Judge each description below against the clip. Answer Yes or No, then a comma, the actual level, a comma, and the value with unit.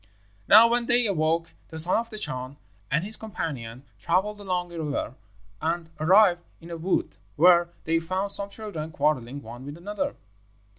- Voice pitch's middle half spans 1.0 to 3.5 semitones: No, average, 4.7 semitones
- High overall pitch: No, medium, 170 Hz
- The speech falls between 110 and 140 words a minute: No, average, 165 wpm